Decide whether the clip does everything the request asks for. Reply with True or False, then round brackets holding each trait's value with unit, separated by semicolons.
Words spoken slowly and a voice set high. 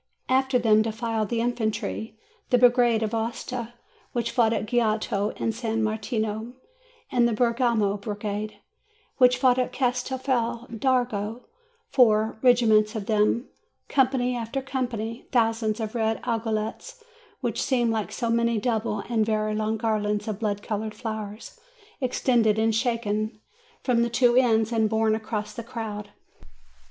False (145 wpm; 225 Hz)